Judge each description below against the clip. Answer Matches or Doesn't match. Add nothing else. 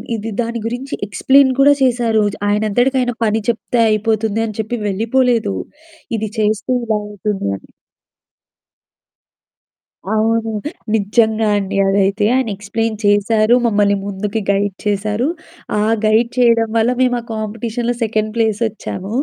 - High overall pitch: Matches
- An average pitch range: Doesn't match